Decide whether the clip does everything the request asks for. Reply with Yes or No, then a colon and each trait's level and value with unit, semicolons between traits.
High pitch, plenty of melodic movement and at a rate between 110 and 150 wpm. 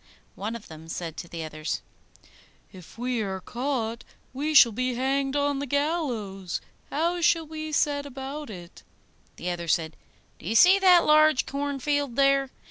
No: very high, 265 Hz; wide, 6.7 semitones; average, 160 wpm